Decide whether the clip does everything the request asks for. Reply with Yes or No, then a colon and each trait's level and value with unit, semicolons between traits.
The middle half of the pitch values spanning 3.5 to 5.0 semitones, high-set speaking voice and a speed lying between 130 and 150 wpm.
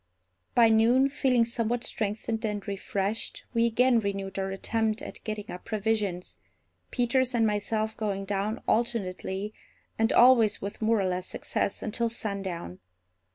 No: average, 2.7 semitones; high, 215 Hz; average, 140 wpm